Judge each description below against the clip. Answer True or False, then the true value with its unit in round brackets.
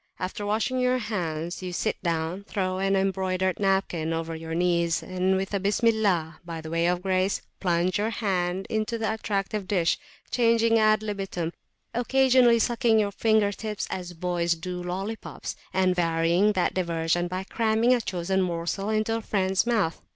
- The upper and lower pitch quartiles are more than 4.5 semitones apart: False (3.7 semitones)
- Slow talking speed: False (160 wpm)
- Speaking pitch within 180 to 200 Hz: True (190 Hz)